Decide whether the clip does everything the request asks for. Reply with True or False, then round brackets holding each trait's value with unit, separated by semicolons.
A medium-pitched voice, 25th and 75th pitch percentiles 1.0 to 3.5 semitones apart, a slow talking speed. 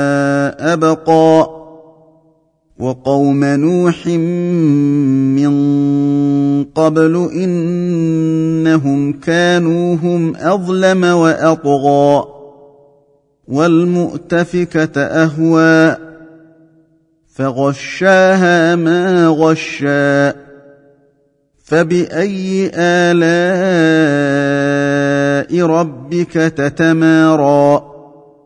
True (160 Hz; 2.9 semitones; 40 wpm)